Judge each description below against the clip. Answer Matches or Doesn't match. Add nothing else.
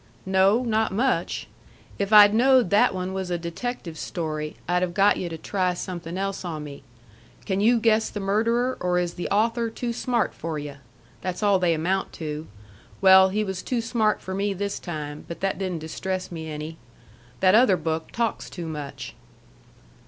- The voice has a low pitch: Doesn't match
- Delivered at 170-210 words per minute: Matches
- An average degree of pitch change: Matches